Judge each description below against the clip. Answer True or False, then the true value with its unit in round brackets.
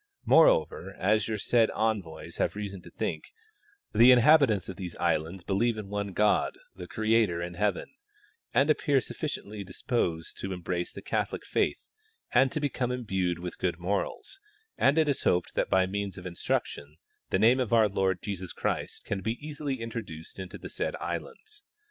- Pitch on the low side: True (100 Hz)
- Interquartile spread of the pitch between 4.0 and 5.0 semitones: True (4.6 semitones)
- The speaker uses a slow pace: False (175 wpm)